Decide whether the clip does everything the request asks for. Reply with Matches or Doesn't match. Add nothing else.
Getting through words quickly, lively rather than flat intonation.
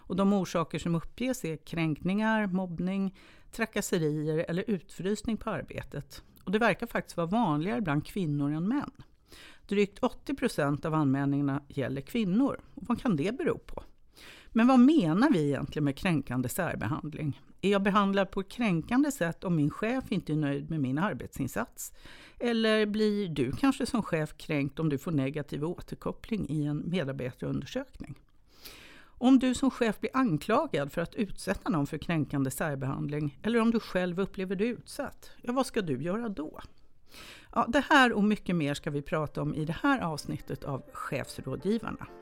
Doesn't match